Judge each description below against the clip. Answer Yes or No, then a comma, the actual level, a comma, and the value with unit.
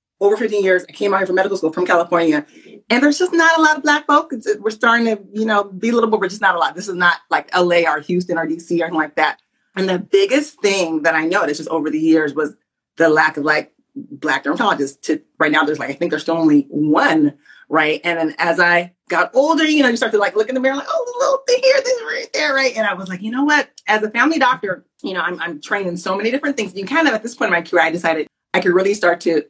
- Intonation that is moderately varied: No, wide, 8.1 semitones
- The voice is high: Yes, high, 195 Hz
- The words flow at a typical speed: No, fast, 285 wpm